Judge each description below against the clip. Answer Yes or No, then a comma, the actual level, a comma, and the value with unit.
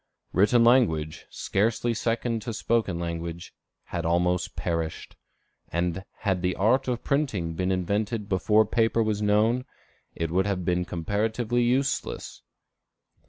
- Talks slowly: Yes, slow, 125 wpm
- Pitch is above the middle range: No, low, 100 Hz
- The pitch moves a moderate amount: Yes, average, 4.7 semitones